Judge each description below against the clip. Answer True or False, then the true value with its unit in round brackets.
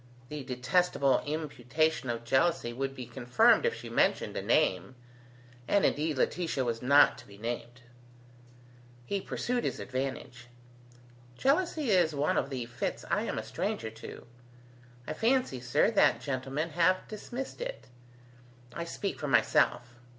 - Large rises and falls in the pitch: True (6.3 semitones)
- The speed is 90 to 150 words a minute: True (145 wpm)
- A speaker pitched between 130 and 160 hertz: True (140 Hz)